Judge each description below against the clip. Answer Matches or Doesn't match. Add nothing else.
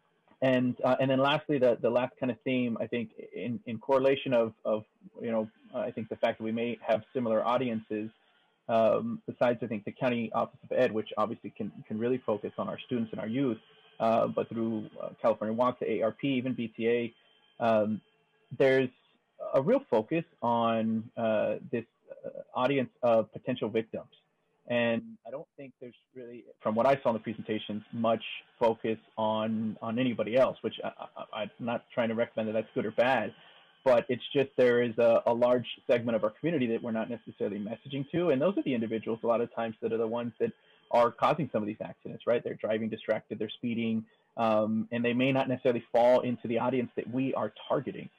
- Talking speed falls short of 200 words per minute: Doesn't match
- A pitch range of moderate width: Doesn't match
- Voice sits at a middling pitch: Doesn't match